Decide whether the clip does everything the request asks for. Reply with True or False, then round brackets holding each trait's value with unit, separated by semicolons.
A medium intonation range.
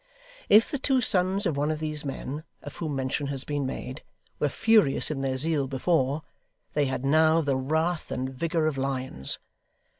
True (3.3 semitones)